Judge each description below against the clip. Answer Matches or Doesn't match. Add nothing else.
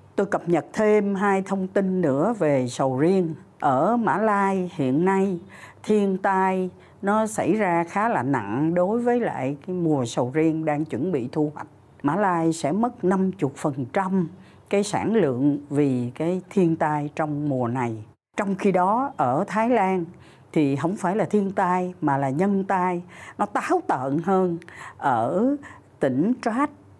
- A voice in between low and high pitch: Matches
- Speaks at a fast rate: Doesn't match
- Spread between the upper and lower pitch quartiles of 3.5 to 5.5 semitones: Matches